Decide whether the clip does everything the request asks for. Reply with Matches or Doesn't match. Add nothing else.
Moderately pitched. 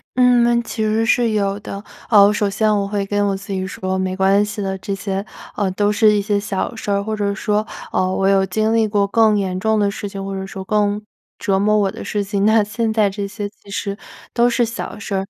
Doesn't match